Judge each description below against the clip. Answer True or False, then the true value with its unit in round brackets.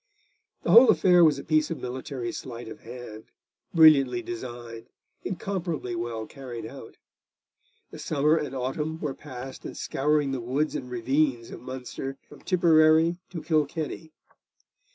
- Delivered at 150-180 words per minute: False (140 wpm)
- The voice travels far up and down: False (4.3 semitones)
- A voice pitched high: False (135 Hz)